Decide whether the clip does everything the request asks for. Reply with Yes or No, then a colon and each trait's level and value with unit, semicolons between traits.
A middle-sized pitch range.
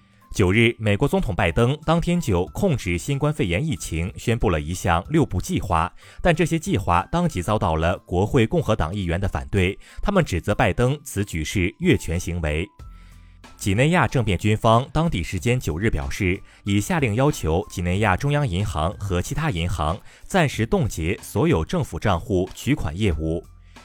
No: wide, 7.2 semitones